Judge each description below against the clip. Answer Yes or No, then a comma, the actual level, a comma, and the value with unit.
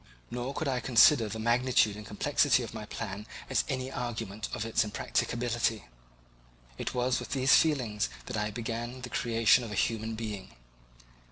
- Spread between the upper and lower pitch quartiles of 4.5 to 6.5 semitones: No, narrow, 2.6 semitones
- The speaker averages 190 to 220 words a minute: No, average, 165 wpm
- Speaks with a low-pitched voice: Yes, low, 115 Hz